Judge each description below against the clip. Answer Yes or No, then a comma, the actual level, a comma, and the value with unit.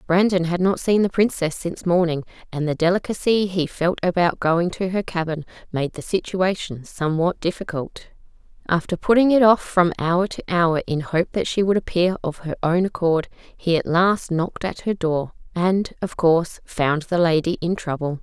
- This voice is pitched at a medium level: Yes, medium, 175 Hz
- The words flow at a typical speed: Yes, average, 185 wpm